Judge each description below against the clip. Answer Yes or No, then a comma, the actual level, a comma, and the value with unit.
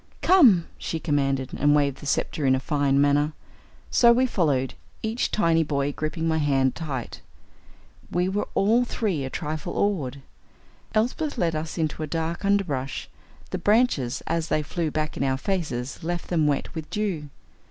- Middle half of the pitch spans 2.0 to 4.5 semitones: No, average, 4.9 semitones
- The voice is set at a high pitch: No, medium, 155 Hz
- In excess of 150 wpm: Yes, average, 165 wpm